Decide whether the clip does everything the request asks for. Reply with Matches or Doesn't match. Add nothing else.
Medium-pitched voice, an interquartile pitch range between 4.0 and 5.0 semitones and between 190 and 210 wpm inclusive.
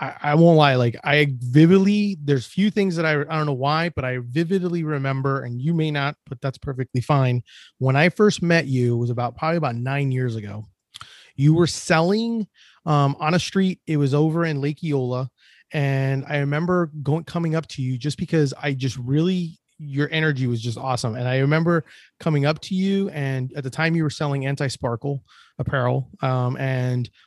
Doesn't match